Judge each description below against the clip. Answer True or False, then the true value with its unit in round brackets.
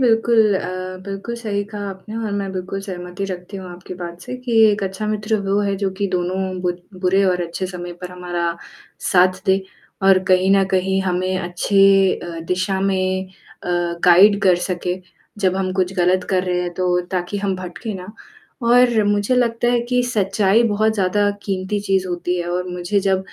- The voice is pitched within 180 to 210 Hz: True (190 Hz)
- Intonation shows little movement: True (2.0 semitones)